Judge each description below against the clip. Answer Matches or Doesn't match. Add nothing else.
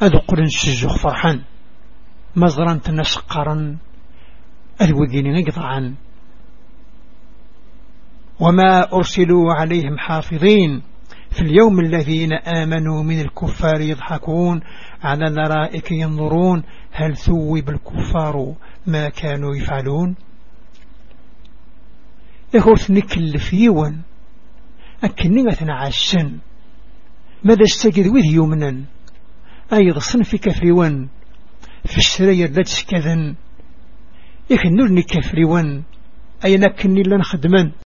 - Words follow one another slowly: Matches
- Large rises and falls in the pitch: Doesn't match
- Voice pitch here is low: Doesn't match